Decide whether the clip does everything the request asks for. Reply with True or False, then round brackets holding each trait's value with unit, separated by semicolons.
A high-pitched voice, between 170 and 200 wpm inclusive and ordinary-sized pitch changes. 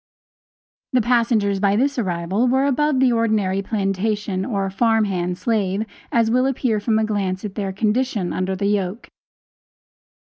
False (210 Hz; 150 wpm; 3.4 semitones)